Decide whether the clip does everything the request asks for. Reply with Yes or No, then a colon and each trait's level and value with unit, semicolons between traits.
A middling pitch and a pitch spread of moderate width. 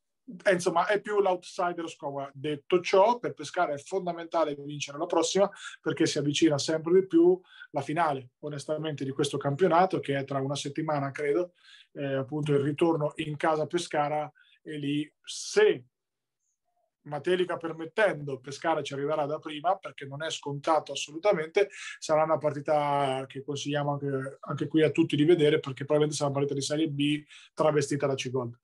Yes: medium, 150 Hz; average, 3.2 semitones